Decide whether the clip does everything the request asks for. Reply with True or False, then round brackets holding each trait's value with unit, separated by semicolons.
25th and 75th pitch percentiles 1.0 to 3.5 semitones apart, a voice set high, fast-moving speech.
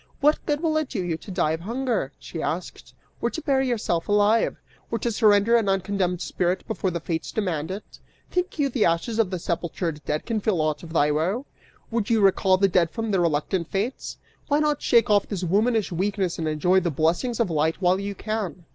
False (4.9 semitones; 195 Hz; 210 wpm)